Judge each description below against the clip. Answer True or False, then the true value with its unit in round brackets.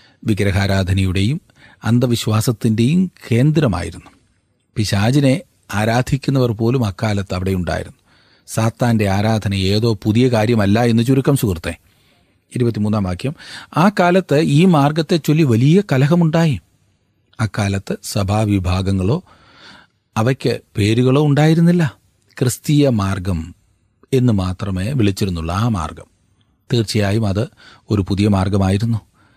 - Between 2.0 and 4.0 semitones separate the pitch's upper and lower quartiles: False (5.0 semitones)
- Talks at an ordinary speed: True (90 wpm)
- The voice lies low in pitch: True (110 Hz)